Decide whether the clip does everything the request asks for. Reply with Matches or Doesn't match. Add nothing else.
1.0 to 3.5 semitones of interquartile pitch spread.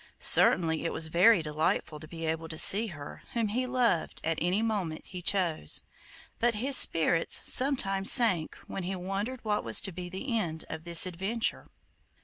Doesn't match